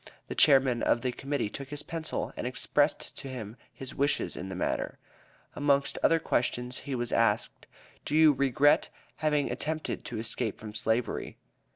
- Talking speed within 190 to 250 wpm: No, average, 165 wpm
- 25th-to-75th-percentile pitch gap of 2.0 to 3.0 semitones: No, average, 3.4 semitones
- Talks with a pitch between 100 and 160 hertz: Yes, low, 135 Hz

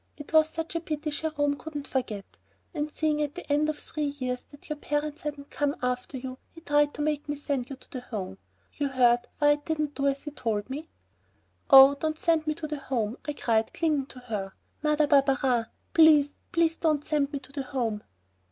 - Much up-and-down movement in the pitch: No, narrow, 2.6 semitones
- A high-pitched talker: Yes, very high, 290 Hz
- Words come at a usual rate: No, fast, 210 wpm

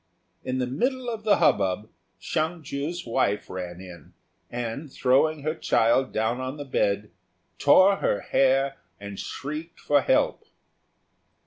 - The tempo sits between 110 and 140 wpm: Yes, slow, 135 wpm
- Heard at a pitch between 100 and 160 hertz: Yes, low, 135 Hz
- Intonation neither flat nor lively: No, wide, 5.9 semitones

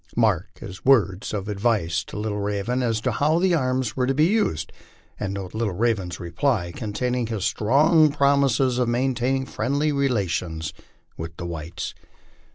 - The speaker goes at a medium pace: Yes, average, 160 wpm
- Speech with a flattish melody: No, wide, 5.5 semitones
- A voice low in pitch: Yes, low, 115 Hz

